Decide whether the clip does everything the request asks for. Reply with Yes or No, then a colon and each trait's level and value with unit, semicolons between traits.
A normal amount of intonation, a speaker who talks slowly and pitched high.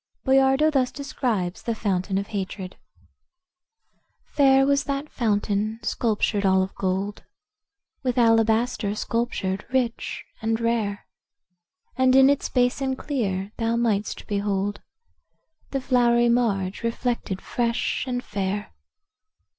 Yes: average, 3.9 semitones; slow, 110 wpm; high, 230 Hz